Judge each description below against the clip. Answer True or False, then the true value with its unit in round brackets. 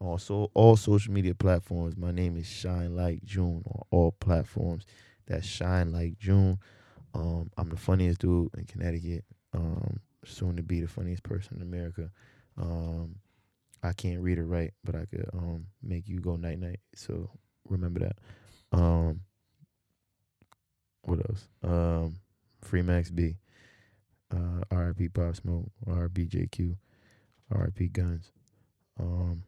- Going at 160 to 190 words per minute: False (140 wpm)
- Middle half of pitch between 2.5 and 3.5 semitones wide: True (3.2 semitones)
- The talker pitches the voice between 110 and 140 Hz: False (90 Hz)